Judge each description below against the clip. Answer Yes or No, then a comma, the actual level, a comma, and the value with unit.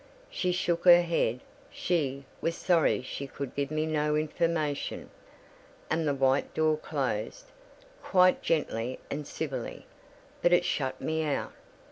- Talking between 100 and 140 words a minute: Yes, slow, 135 wpm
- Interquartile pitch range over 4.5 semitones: No, average, 3.4 semitones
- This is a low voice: No, medium, 155 Hz